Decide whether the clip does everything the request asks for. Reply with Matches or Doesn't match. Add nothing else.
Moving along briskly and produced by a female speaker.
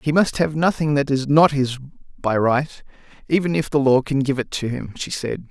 Doesn't match